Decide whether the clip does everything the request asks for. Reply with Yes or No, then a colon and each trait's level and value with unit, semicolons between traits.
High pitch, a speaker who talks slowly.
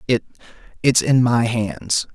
No: low, 120 Hz; slow, 110 wpm